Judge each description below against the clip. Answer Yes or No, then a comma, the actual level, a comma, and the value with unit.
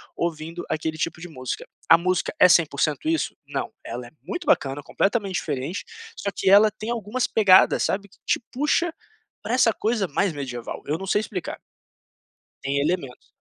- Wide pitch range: Yes, wide, 5.8 semitones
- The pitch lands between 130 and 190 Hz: Yes, medium, 185 Hz